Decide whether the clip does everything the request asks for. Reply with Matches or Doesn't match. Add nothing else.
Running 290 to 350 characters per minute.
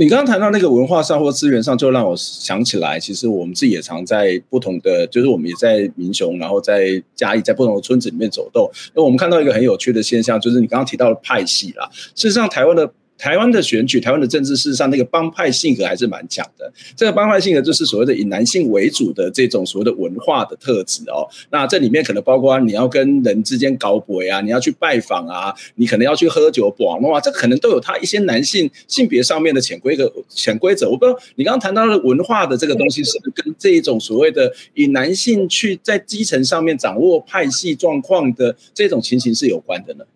Doesn't match